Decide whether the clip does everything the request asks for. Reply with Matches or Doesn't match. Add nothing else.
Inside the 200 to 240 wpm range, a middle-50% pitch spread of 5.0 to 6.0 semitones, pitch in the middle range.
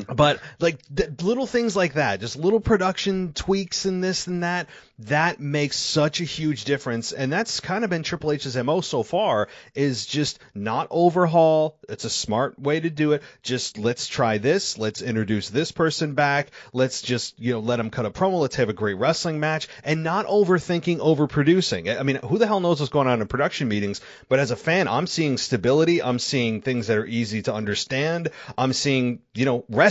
Matches